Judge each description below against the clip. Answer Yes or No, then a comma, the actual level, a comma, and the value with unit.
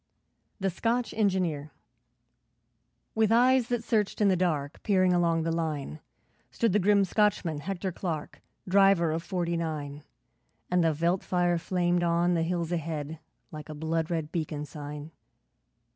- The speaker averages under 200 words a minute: Yes, average, 145 wpm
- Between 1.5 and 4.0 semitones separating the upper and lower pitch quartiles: Yes, average, 3.4 semitones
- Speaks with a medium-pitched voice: Yes, medium, 170 Hz